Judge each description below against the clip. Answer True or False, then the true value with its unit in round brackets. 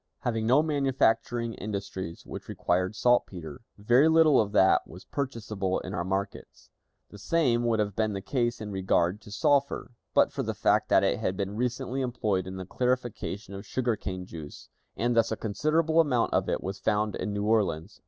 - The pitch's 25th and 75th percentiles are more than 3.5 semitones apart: True (4.3 semitones)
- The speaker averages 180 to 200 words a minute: True (185 wpm)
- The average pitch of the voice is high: False (110 Hz)